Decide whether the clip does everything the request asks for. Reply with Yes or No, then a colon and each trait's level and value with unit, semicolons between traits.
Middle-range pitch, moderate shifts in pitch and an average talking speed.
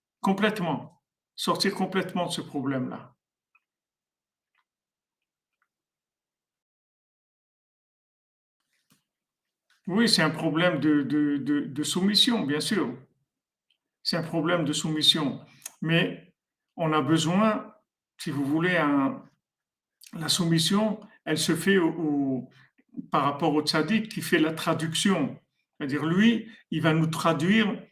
No: medium, 165 Hz; average, 4.4 semitones; slow, 110 wpm